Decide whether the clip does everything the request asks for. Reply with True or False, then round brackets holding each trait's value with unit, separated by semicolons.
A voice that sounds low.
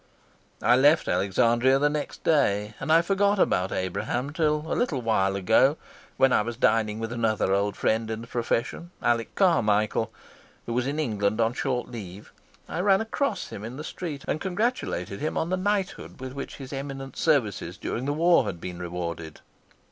True (125 Hz)